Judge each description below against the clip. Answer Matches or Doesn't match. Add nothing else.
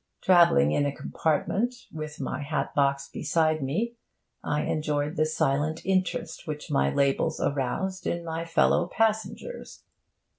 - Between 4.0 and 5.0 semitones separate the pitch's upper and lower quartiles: Doesn't match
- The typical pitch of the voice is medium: Matches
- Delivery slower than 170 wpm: Matches